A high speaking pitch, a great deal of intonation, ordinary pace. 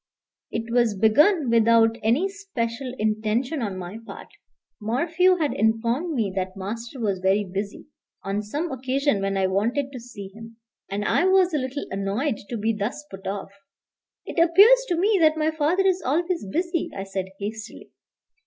Yes: high, 230 Hz; wide, 7.2 semitones; average, 170 wpm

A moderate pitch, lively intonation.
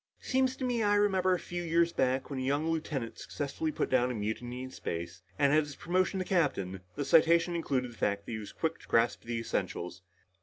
Yes: medium, 145 Hz; wide, 6.4 semitones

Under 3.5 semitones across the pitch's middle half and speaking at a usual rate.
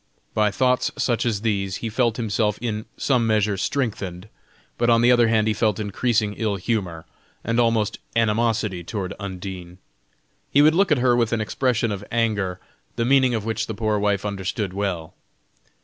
Yes: average, 2.9 semitones; average, 175 wpm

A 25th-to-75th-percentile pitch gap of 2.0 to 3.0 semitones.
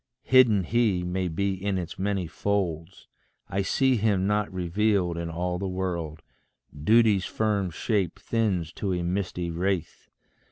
Yes: average, 2.7 semitones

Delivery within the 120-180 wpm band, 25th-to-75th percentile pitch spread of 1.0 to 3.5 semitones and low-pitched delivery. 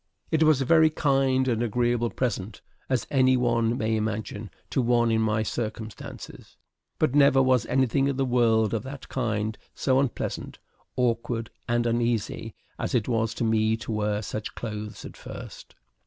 Yes: average, 165 wpm; average, 2.8 semitones; low, 120 Hz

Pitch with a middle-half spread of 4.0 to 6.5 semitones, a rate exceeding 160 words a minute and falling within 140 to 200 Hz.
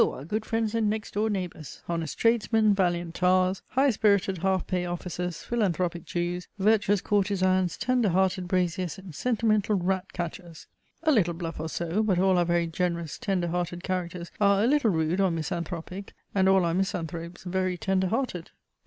No: average, 2.9 semitones; average, 170 wpm; medium, 185 Hz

